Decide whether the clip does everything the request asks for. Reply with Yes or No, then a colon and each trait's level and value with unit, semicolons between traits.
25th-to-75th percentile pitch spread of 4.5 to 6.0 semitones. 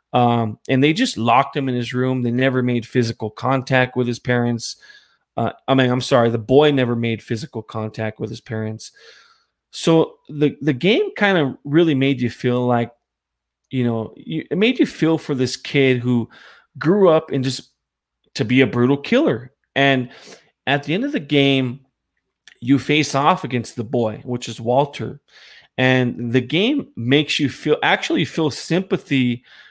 No: average, 3.3 semitones